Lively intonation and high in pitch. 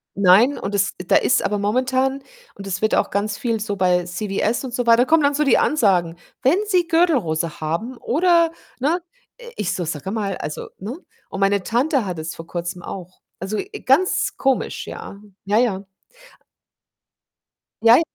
Yes: wide, 6.1 semitones; high, 215 Hz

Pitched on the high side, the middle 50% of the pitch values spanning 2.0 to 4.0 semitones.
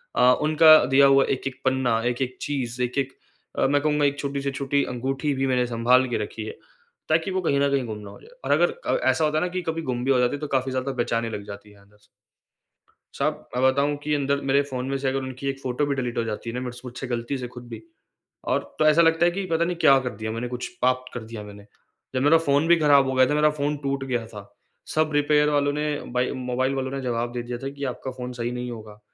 No: low, 130 Hz; average, 2.7 semitones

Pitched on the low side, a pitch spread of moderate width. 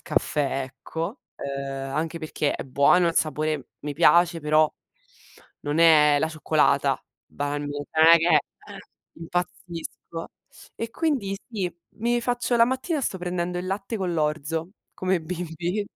No: medium, 165 Hz; average, 3.7 semitones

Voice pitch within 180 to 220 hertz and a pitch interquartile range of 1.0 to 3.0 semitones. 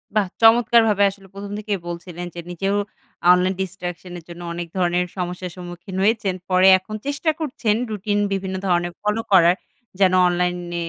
Yes: medium, 185 Hz; average, 2.7 semitones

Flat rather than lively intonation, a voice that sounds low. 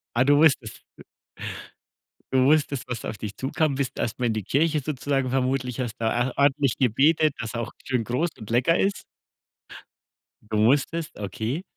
No: average, 3.6 semitones; low, 130 Hz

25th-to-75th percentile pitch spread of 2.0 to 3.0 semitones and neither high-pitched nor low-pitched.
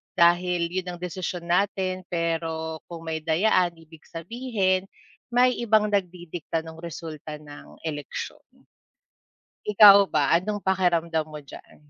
Yes: average, 2.7 semitones; medium, 175 Hz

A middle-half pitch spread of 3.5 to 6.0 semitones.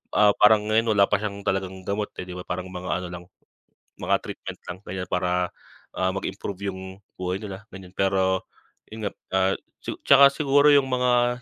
No: average, 2.7 semitones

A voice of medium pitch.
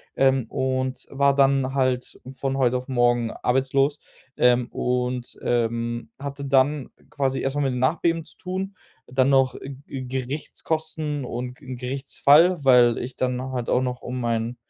No: low, 130 Hz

